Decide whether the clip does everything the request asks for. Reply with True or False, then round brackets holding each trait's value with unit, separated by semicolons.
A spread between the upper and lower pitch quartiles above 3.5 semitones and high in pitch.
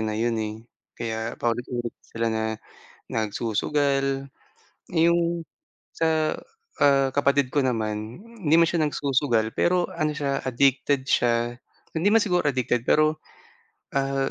False (4.4 semitones; 135 Hz)